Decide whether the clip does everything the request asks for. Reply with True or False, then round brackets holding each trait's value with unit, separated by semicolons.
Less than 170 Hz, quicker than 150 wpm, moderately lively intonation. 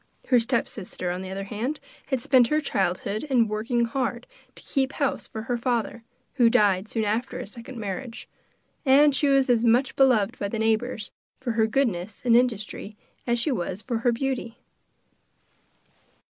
False (235 Hz; 170 wpm; 3.2 semitones)